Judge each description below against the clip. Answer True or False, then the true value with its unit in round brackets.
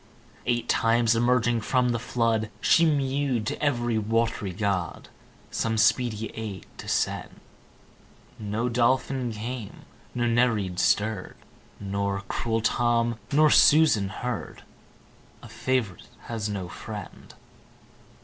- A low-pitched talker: True (115 Hz)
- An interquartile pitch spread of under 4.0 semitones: True (2.7 semitones)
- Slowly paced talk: True (110 wpm)